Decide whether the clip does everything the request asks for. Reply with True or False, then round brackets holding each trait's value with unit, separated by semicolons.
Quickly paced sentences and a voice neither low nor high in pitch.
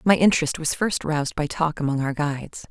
True (220 wpm; 155 Hz)